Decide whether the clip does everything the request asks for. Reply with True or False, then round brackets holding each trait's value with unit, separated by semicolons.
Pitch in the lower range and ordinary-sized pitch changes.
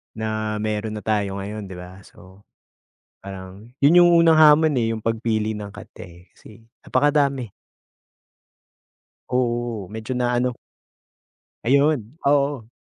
True (110 Hz; 4.6 semitones)